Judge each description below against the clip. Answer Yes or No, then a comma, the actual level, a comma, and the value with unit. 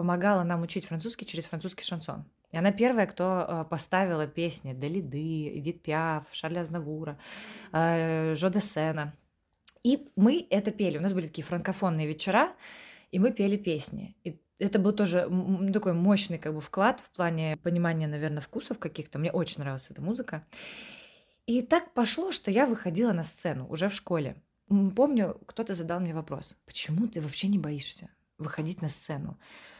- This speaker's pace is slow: No, average, 155 wpm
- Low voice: No, medium, 175 Hz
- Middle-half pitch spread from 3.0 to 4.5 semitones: Yes, average, 4.2 semitones